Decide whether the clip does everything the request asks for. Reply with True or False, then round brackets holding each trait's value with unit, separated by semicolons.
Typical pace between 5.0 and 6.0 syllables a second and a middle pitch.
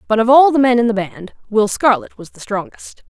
False (5.4 syllables/s; 225 Hz)